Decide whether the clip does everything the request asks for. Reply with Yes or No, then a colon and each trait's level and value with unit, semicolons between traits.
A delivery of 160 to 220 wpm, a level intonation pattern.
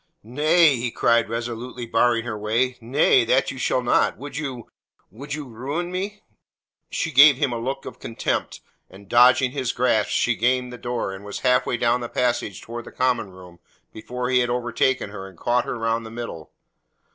Yes: average, 190 wpm; narrow, 2.1 semitones